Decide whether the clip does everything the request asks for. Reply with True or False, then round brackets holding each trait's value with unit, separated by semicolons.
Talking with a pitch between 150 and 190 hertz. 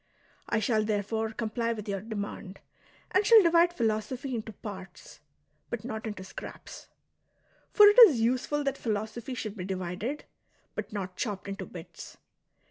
False (220 Hz)